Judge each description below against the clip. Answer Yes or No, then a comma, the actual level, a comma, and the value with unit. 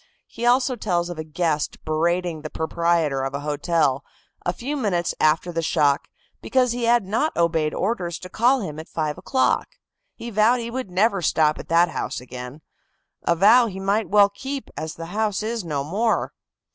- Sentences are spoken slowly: No, average, 185 wpm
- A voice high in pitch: No, medium, 175 Hz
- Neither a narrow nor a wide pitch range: No, wide, 6.1 semitones